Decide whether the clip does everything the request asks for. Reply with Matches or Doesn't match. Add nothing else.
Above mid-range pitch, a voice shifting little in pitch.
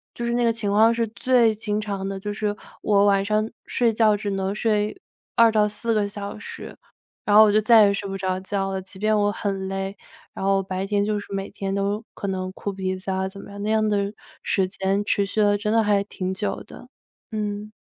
Matches